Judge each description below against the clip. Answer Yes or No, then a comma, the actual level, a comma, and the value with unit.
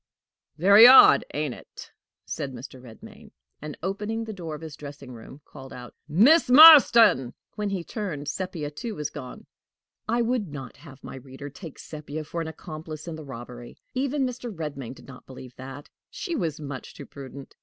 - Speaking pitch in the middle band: Yes, medium, 155 Hz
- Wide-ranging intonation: Yes, wide, 7.4 semitones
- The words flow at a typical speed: Yes, average, 175 wpm